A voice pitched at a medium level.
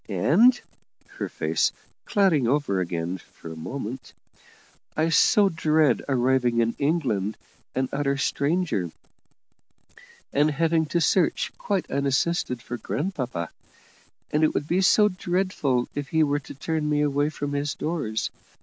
Yes: medium, 145 Hz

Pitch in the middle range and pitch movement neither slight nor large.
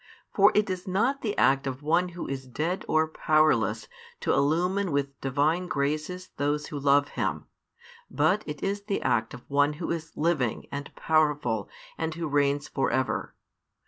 Yes: medium, 155 Hz; average, 4.1 semitones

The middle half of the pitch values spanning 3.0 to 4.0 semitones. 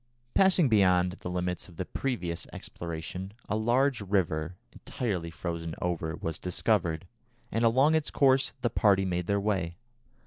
No: average, 5.0 semitones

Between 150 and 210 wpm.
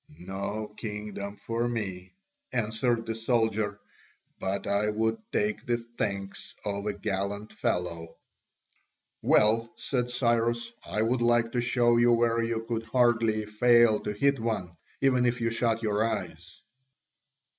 No: slow, 135 wpm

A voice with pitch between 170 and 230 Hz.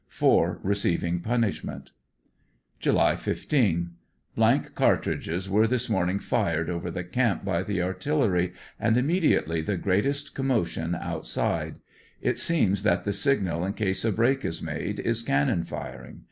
No: low, 100 Hz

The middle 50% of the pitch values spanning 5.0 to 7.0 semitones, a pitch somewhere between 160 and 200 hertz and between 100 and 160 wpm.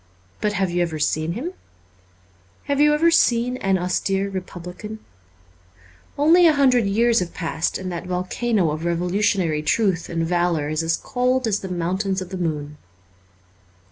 Yes: wide, 5.4 semitones; medium, 185 Hz; average, 155 wpm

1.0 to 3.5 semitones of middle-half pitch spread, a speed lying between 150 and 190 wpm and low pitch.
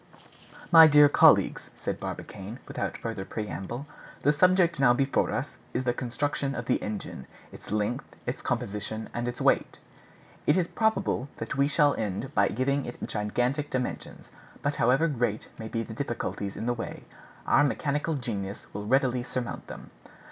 No: average, 4.4 semitones; average, 160 wpm; low, 125 Hz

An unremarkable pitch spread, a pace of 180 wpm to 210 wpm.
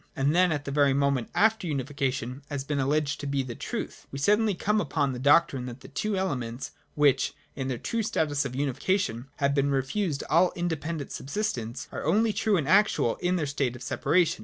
Yes: average, 4.7 semitones; average, 200 wpm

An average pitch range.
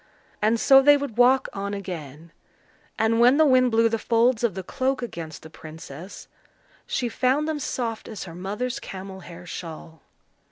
No: wide, 6.1 semitones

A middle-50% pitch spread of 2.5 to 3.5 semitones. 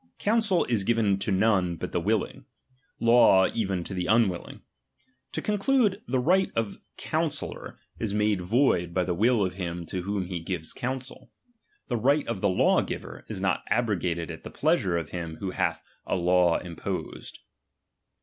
No: average, 4.7 semitones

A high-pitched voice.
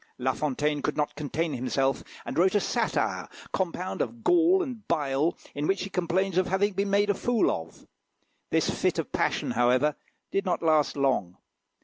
No: medium, 170 Hz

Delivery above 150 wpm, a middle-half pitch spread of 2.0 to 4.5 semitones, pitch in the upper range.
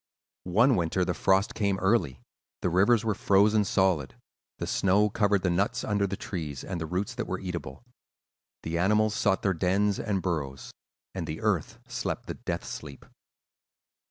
No: average, 165 wpm; average, 3.0 semitones; very low, 95 Hz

